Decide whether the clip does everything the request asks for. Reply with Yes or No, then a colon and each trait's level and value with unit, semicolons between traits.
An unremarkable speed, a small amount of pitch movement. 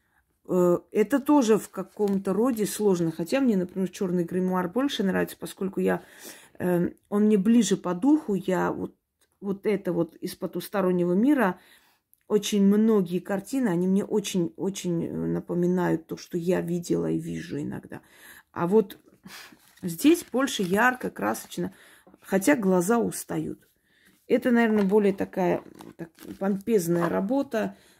No: average, 120 wpm; average, 3.4 semitones